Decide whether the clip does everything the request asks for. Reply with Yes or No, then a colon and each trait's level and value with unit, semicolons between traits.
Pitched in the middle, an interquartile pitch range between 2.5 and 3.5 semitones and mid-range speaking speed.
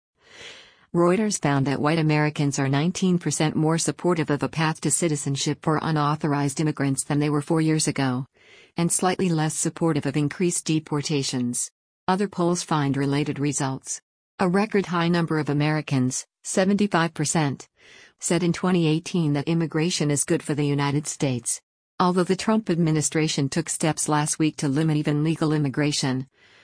Yes: medium, 155 Hz; average, 2.8 semitones; average, 150 wpm